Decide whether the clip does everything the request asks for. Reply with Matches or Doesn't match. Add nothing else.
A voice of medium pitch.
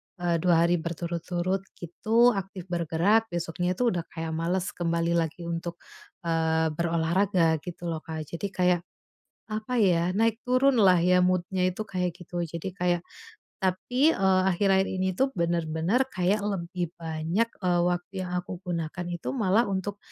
Matches